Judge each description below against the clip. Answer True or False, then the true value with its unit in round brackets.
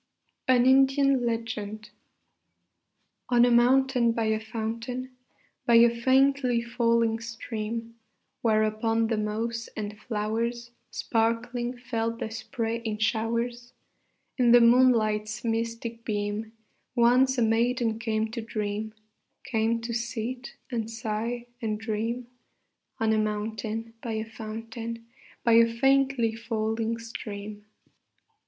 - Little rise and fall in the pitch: True (1.6 semitones)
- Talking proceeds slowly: True (115 wpm)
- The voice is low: False (230 Hz)